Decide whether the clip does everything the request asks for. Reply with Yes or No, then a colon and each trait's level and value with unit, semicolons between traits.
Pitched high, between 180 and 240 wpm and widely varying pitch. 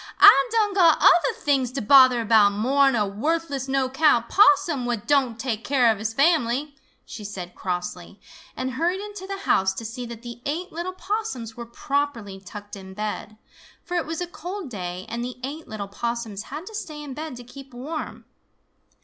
Yes: very high, 255 Hz; average, 185 wpm; wide, 6.5 semitones